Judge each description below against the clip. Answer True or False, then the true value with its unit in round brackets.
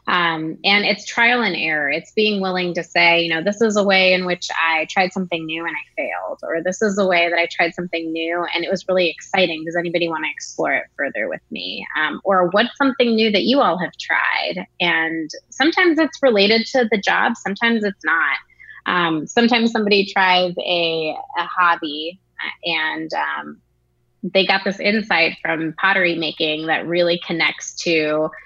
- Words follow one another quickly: False (190 wpm)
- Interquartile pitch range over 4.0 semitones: False (3.7 semitones)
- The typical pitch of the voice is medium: True (175 Hz)